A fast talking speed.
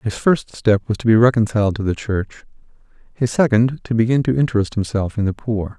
Yes: fast, 210 wpm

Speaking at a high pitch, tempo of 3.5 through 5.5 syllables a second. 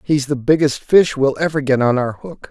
No: medium, 140 Hz; 5.0 syllables/s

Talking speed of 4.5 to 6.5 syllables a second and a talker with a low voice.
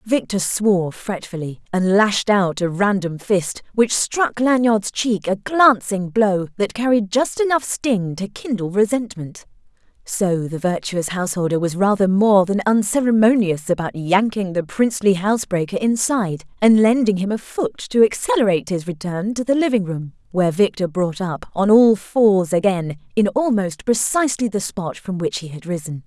No: 4.7 syllables/s; high, 200 Hz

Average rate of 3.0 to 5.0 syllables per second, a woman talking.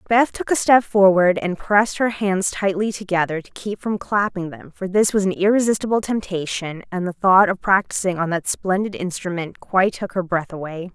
No: 5.2 syllables/s; female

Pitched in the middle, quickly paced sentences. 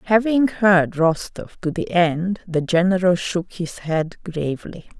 No: medium, 180 Hz; average, 145 wpm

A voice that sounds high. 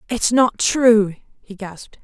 Yes: high, 220 Hz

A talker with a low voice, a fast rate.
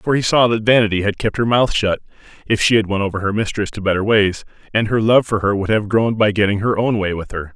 Yes: low, 105 Hz; fast, 280 wpm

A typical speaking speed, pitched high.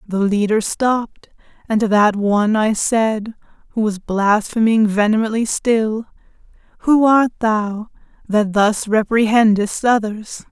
No: slow, 120 wpm; high, 215 Hz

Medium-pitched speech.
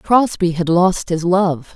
Yes: medium, 180 Hz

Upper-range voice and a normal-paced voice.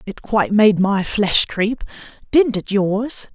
Yes: high, 210 Hz; average, 160 wpm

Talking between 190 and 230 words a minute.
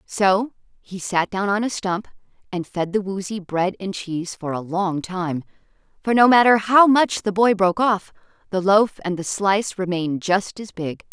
Yes: average, 195 wpm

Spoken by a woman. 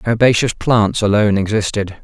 No: male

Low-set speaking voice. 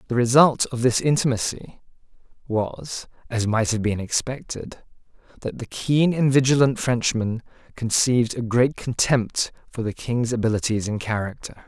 Yes: low, 120 Hz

